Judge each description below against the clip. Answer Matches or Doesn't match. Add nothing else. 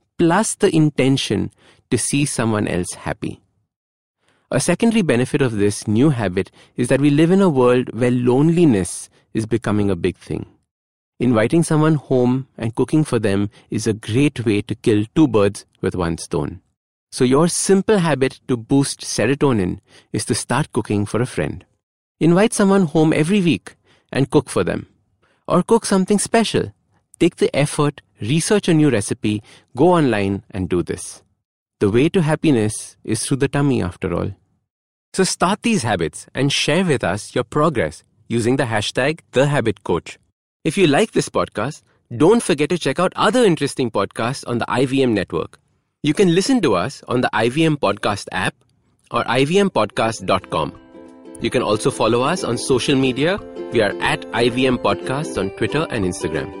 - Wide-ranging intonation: Matches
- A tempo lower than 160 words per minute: Doesn't match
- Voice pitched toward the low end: Matches